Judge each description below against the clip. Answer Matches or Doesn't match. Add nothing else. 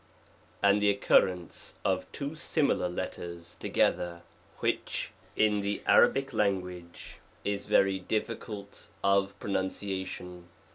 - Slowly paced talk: Matches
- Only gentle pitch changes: Matches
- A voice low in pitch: Matches